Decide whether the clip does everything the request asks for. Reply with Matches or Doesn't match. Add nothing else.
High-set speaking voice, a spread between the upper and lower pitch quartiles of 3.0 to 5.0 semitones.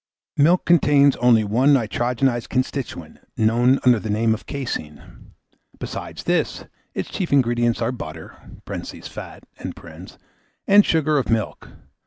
Doesn't match